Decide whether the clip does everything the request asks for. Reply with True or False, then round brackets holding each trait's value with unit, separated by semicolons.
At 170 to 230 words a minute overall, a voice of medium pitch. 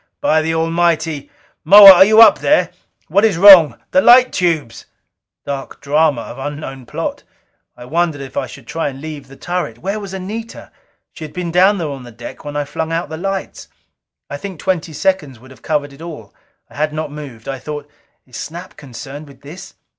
True (200 wpm; 155 Hz)